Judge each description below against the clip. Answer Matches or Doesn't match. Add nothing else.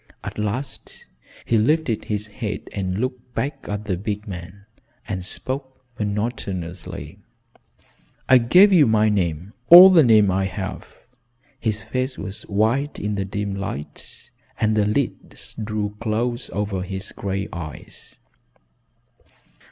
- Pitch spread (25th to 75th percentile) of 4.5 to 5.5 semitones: Doesn't match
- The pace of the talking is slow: Matches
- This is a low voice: Matches